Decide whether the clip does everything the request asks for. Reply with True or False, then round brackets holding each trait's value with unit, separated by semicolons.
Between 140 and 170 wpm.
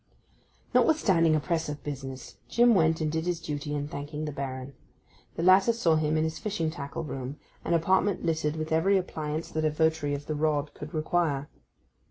False (190 wpm)